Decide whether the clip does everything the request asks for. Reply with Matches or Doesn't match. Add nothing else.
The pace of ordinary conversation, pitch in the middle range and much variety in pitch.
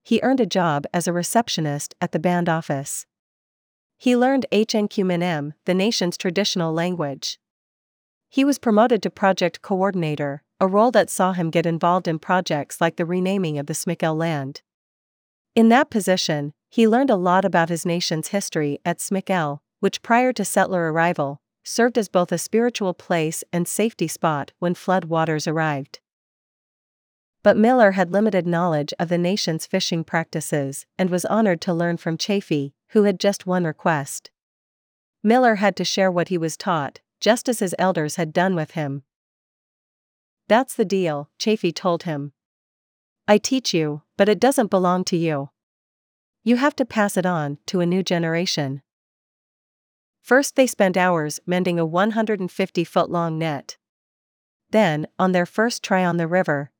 Doesn't match